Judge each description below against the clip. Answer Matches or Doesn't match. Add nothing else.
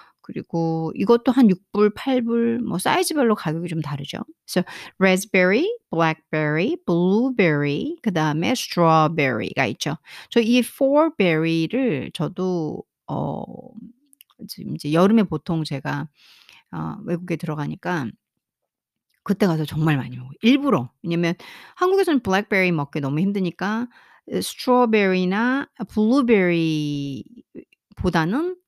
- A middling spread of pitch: Doesn't match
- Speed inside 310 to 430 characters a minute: Doesn't match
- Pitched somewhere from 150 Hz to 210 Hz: Matches